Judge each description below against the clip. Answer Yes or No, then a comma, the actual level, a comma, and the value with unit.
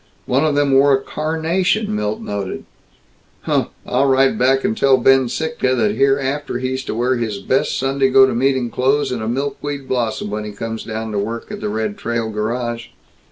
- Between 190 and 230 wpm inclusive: Yes, average, 195 wpm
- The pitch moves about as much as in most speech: Yes, average, 3.5 semitones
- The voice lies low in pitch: Yes, low, 130 Hz